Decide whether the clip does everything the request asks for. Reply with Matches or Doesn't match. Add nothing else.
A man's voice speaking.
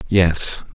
Matches